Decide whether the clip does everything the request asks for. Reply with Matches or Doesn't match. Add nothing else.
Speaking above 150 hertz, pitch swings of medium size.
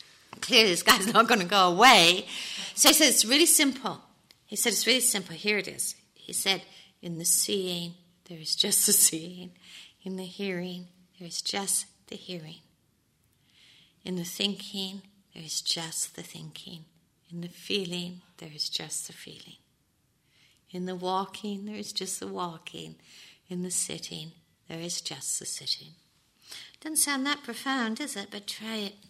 Matches